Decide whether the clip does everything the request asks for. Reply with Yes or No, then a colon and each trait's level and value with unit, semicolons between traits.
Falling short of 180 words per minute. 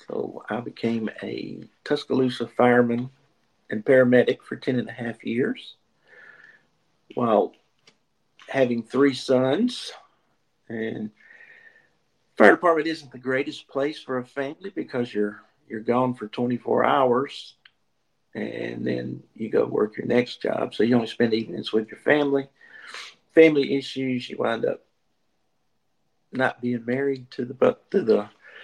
Yes: slow, 135 wpm